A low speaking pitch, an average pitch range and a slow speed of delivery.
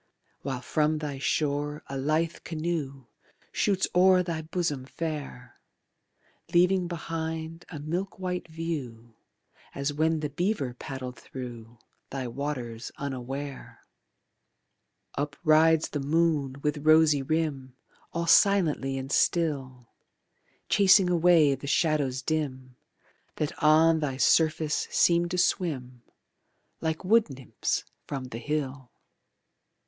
No: medium, 150 Hz; average, 3.6 semitones; slow, 110 wpm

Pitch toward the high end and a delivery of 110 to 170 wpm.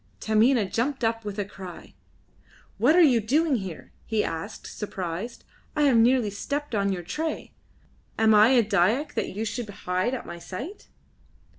Yes: high, 220 Hz; average, 165 wpm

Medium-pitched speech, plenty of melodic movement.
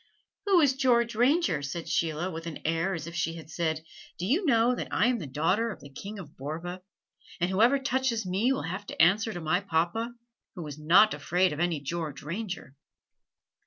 Yes: medium, 180 Hz; wide, 6.0 semitones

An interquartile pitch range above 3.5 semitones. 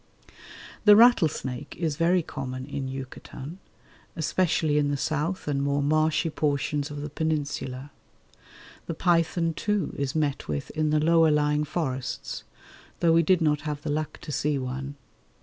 No: narrow, 2.5 semitones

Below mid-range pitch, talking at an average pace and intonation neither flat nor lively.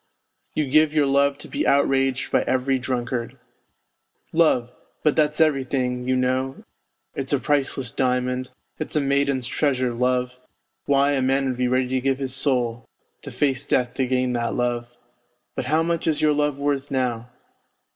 No: low, 130 Hz; average, 165 wpm; narrow, 2.0 semitones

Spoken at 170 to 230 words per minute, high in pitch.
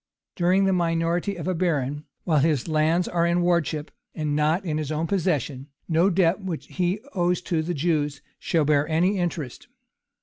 No: average, 180 wpm; medium, 165 Hz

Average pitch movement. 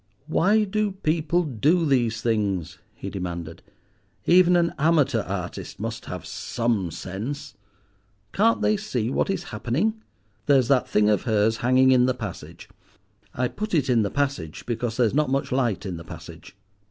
No: wide, 7.2 semitones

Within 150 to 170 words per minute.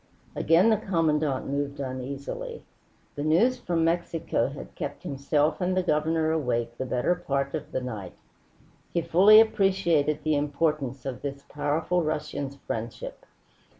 No: average, 140 wpm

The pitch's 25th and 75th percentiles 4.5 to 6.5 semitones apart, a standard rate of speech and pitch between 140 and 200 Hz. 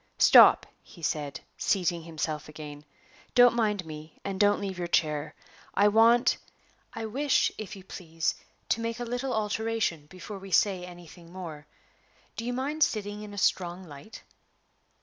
Yes: average, 5.2 semitones; average, 155 wpm; high, 190 Hz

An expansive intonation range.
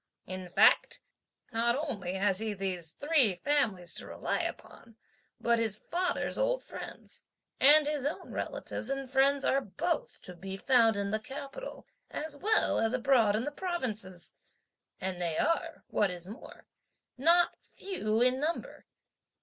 Yes: wide, 6.6 semitones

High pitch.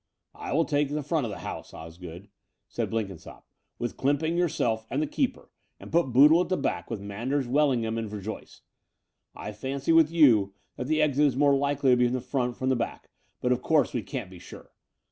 No: low, 130 Hz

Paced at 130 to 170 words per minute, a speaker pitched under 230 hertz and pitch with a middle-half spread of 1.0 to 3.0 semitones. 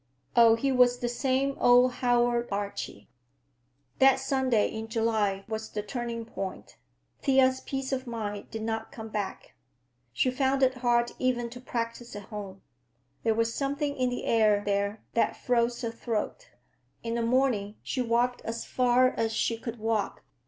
No: average, 160 wpm; high, 235 Hz; narrow, 2.4 semitones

